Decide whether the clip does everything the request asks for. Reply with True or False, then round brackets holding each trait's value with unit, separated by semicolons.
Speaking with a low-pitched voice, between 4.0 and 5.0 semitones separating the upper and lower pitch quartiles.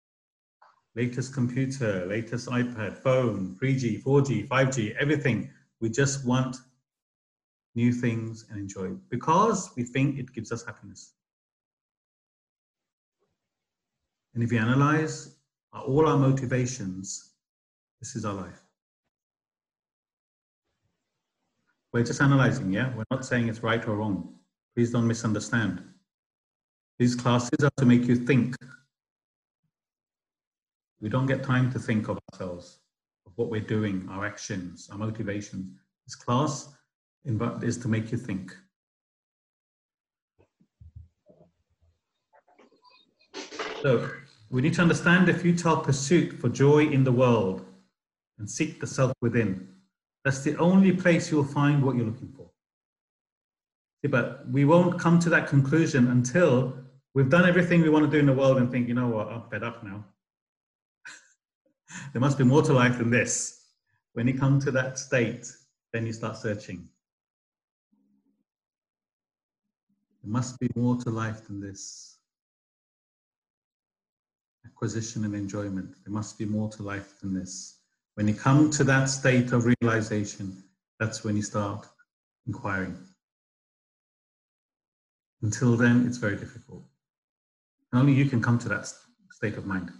True (120 Hz; 4.5 semitones)